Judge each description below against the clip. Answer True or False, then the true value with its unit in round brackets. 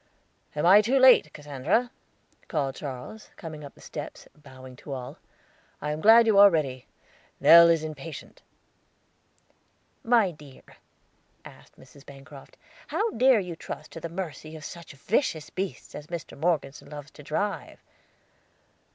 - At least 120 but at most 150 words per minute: True (145 wpm)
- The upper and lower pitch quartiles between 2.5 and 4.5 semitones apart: False (5.5 semitones)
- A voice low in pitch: False (155 Hz)